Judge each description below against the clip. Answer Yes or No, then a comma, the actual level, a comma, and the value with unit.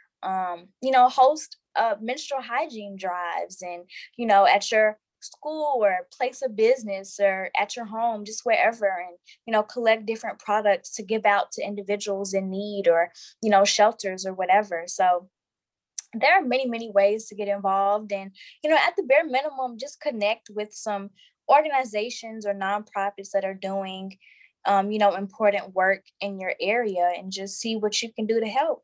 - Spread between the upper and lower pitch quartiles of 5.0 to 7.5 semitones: No, average, 3.2 semitones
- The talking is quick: No, average, 180 wpm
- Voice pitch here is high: Yes, high, 210 Hz